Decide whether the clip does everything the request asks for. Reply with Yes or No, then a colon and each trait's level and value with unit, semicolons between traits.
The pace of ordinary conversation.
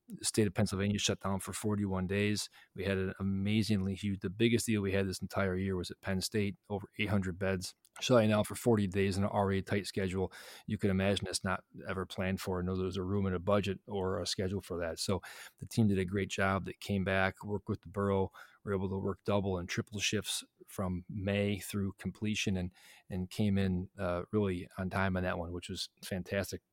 No: fast, 225 wpm